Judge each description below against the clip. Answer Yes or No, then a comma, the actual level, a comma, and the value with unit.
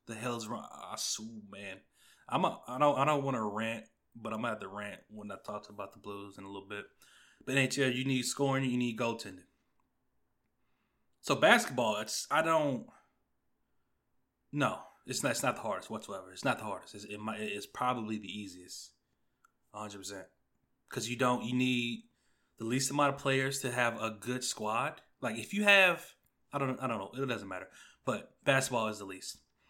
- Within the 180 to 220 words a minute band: Yes, average, 195 wpm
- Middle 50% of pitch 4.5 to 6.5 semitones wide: No, average, 3.7 semitones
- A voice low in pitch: Yes, low, 115 Hz